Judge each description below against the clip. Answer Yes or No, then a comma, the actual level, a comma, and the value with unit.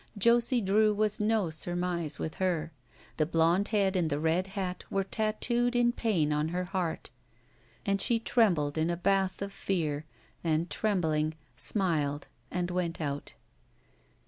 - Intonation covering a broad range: No, average, 4.3 semitones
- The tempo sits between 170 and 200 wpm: No, average, 145 wpm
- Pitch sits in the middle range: Yes, medium, 180 Hz